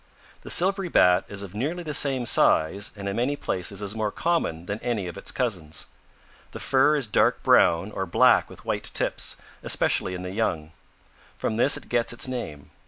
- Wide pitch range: Yes, wide, 6.3 semitones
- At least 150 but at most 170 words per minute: No, average, 185 wpm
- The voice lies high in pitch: No, low, 105 Hz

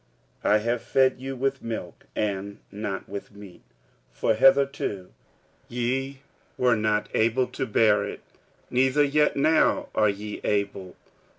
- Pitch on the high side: No, low, 115 Hz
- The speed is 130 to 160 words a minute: Yes, slow, 135 wpm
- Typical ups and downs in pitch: Yes, average, 4.4 semitones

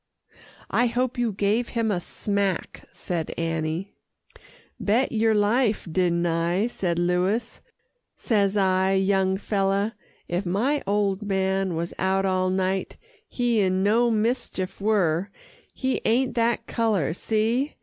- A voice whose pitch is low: No, high, 200 Hz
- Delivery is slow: Yes, slow, 130 wpm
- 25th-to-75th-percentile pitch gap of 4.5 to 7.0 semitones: No, average, 3.3 semitones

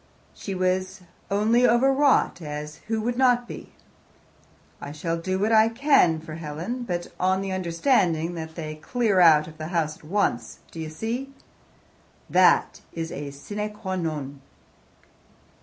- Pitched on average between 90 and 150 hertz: No, medium, 185 Hz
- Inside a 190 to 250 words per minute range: No, average, 155 wpm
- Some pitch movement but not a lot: No, wide, 5.9 semitones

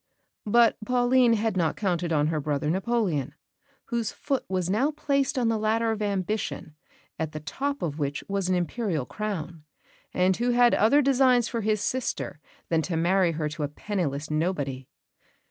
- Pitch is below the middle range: No, high, 195 Hz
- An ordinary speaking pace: Yes, average, 170 wpm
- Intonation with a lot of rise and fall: Yes, wide, 6.6 semitones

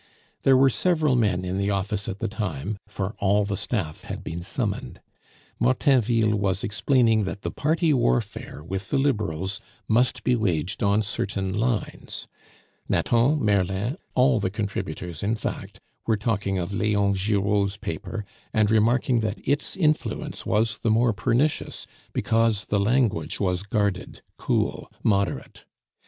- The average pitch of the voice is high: No, low, 105 Hz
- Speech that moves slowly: No, average, 145 wpm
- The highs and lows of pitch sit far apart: No, average, 3.3 semitones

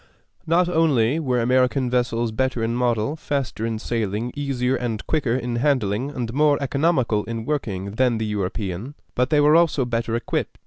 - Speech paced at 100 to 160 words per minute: No, average, 170 wpm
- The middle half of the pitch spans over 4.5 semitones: No, average, 3.8 semitones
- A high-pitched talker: No, low, 125 Hz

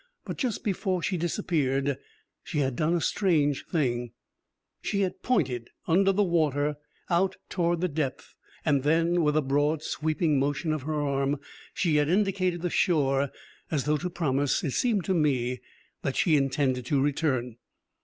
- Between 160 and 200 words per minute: Yes, average, 165 wpm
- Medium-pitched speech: Yes, medium, 150 Hz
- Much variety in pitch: No, average, 4.0 semitones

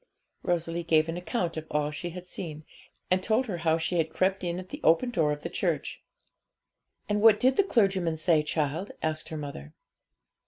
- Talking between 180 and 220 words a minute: Yes, average, 195 wpm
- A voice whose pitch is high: No, medium, 170 Hz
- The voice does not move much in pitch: No, average, 3.1 semitones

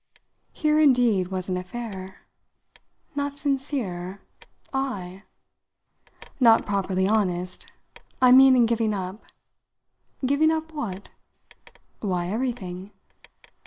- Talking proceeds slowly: Yes, slow, 90 wpm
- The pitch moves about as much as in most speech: No, wide, 6.2 semitones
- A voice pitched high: Yes, high, 220 Hz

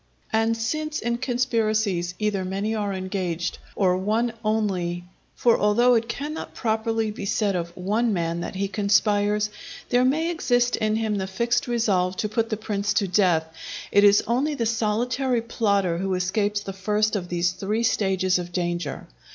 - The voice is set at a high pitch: Yes, high, 210 Hz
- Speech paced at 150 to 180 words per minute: Yes, average, 170 wpm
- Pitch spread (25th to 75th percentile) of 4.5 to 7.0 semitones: No, average, 3.5 semitones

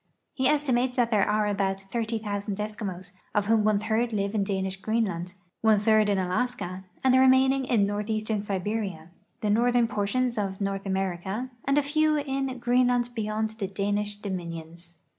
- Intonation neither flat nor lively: Yes, average, 3.8 semitones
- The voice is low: No, high, 210 Hz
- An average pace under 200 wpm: Yes, average, 160 wpm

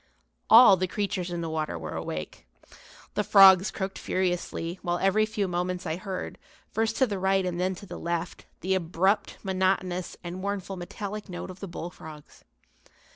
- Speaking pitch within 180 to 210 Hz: Yes, medium, 185 Hz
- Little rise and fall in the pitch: Yes, narrow, 2.0 semitones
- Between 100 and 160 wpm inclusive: No, average, 170 wpm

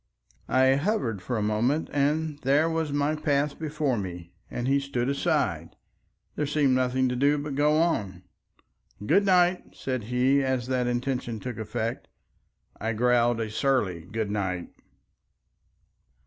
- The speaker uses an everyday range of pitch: Yes, average, 4.3 semitones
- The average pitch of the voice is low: Yes, low, 130 Hz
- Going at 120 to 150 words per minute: Yes, average, 145 wpm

